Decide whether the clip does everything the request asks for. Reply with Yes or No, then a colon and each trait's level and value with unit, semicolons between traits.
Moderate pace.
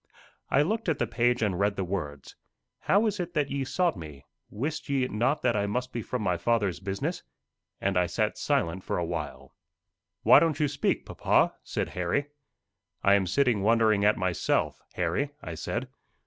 Yes: average, 185 wpm